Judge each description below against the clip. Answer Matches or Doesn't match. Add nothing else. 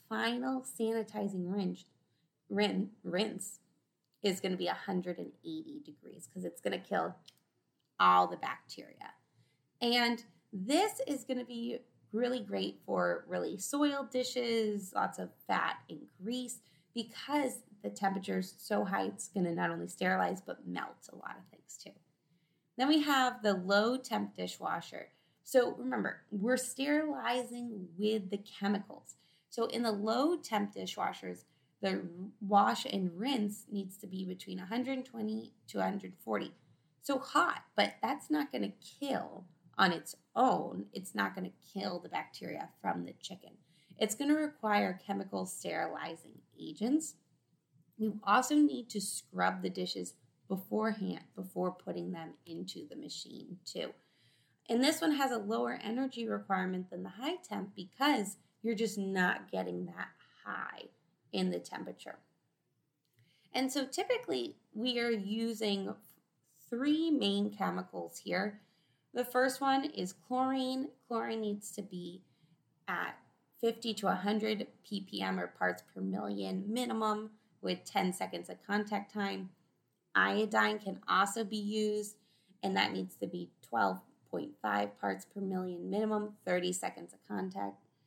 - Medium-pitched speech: Doesn't match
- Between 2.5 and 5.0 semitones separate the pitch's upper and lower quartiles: Doesn't match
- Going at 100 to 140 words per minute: Matches